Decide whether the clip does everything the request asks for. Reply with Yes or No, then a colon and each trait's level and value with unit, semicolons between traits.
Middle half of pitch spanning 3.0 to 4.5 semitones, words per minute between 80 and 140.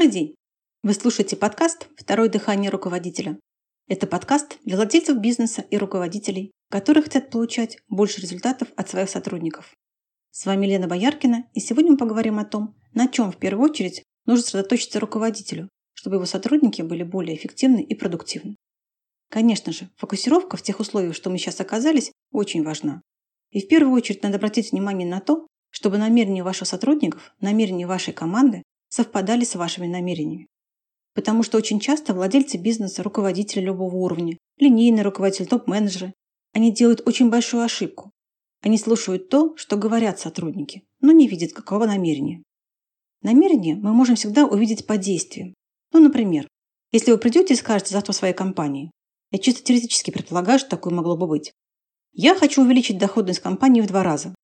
No: average, 4.1 semitones; average, 155 wpm